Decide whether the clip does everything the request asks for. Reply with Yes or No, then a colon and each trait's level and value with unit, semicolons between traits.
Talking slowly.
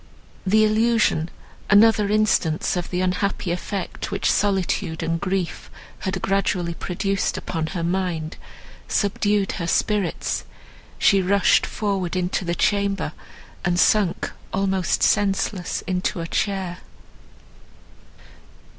Yes: slow, 110 wpm